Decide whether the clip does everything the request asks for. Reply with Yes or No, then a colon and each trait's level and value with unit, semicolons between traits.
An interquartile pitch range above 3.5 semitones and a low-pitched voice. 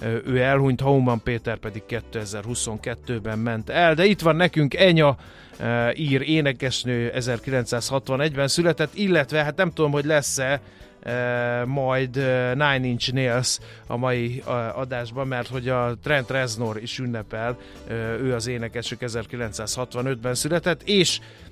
No: average, 2.9 semitones; low, 125 Hz